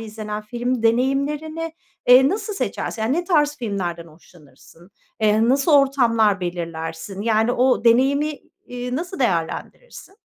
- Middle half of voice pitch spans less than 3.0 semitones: No, average, 5.3 semitones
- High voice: Yes, high, 240 Hz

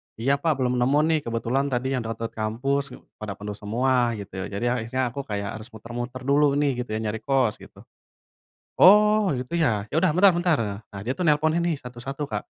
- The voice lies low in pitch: Yes, low, 125 Hz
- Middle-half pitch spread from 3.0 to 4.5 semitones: Yes, average, 4.2 semitones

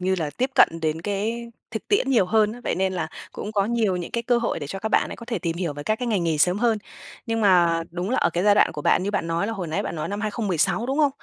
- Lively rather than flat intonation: No, average, 4.8 semitones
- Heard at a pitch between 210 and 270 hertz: No, high, 200 Hz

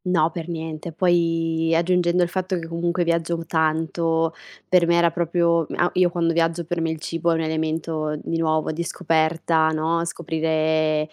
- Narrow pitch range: Yes, narrow, 1.2 semitones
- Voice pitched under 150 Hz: No, medium, 165 Hz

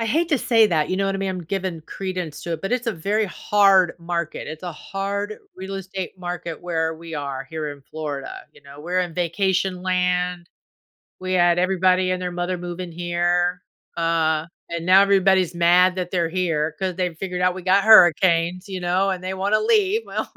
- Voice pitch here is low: No, medium, 180 Hz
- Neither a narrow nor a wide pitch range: No, narrow, 2.1 semitones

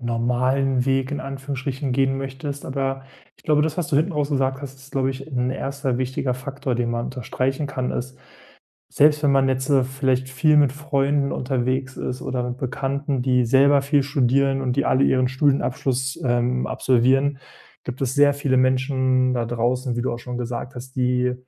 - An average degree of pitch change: No, narrow, 1.6 semitones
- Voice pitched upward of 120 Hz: Yes, low, 130 Hz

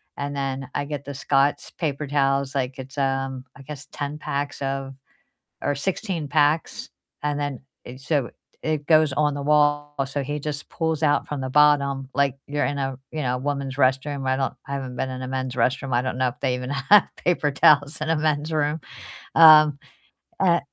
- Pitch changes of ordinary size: No, narrow, 1.8 semitones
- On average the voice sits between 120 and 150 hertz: Yes, medium, 140 Hz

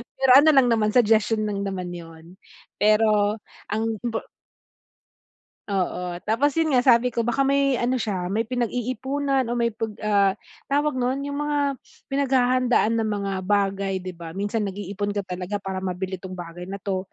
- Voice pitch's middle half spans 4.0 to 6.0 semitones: Yes, average, 4.7 semitones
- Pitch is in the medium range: No, high, 215 Hz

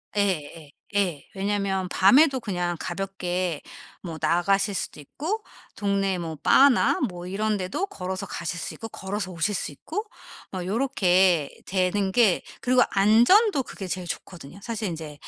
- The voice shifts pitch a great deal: No, average, 3.1 semitones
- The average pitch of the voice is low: No, high, 195 Hz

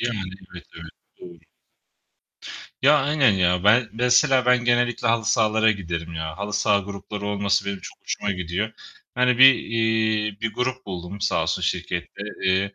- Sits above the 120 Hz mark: No, low, 105 Hz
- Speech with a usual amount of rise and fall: Yes, average, 4.0 semitones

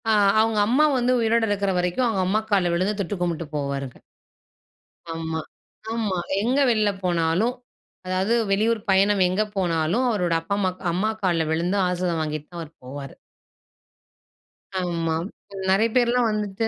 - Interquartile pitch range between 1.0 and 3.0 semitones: No, average, 4.2 semitones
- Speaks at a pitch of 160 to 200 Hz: Yes, medium, 185 Hz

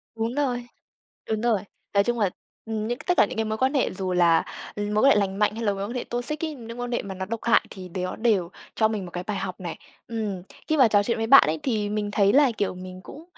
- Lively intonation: No, average, 3.7 semitones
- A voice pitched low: No, high, 215 Hz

